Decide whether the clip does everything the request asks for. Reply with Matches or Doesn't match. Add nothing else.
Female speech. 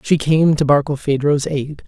Doesn't match